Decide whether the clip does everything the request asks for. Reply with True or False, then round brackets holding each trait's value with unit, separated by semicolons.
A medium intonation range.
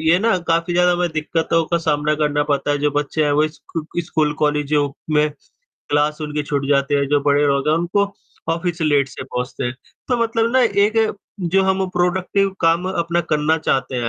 True (3.1 semitones)